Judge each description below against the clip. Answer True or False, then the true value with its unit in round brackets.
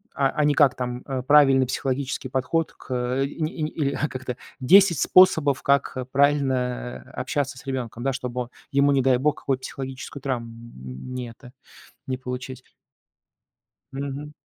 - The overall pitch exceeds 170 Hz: False (130 Hz)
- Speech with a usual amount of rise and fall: False (1.9 semitones)